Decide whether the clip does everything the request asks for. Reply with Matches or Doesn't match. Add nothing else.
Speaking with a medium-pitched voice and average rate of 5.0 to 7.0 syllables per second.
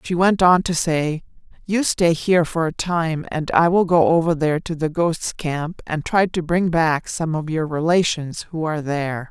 Doesn't match